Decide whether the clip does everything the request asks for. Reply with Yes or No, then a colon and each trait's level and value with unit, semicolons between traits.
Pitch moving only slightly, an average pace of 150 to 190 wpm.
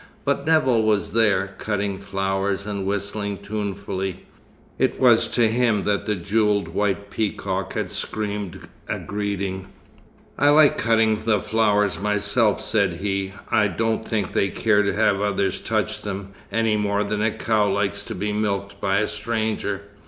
Yes: narrow, 1.6 semitones; average, 155 wpm